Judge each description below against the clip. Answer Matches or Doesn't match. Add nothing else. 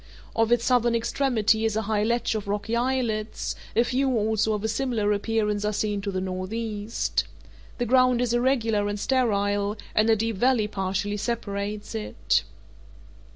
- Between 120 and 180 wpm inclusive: Matches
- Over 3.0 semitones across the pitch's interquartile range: Doesn't match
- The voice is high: Matches